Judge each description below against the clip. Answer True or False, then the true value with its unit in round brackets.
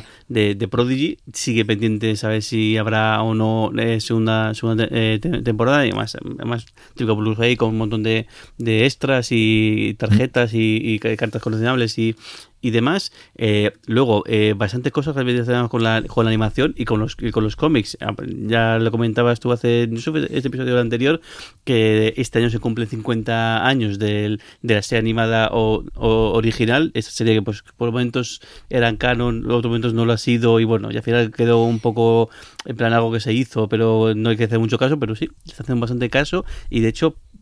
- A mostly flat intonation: True (1.5 semitones)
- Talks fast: True (200 wpm)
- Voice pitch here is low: True (115 Hz)